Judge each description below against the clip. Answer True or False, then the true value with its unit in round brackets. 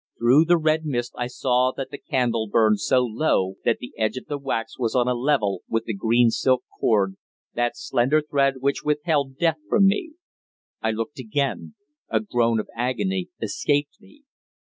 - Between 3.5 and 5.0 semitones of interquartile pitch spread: True (4.2 semitones)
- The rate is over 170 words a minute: True (180 wpm)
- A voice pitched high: False (125 Hz)